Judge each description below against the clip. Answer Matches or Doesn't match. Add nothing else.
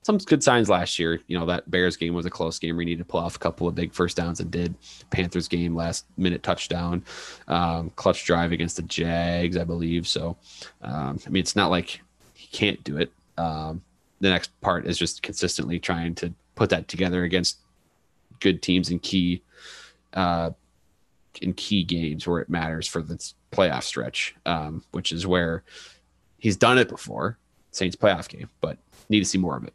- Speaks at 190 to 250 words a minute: Matches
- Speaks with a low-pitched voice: Matches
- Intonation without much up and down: Matches